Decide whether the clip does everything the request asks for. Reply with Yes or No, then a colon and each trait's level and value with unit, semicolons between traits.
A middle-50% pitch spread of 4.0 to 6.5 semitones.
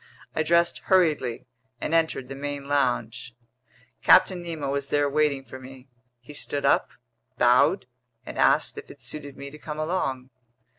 No: average, 2.8 semitones